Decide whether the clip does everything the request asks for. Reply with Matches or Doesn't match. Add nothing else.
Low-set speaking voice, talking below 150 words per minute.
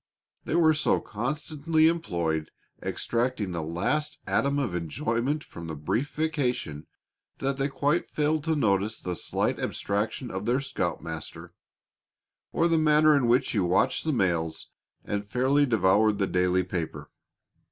Matches